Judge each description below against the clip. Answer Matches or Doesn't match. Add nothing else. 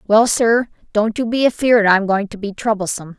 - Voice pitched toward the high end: Matches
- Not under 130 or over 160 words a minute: Doesn't match